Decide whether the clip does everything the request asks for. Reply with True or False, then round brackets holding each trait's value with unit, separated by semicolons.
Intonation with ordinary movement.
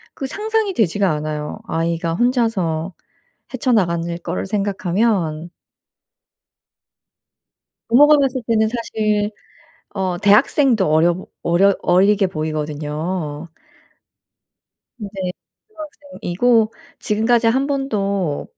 False (5.8 semitones)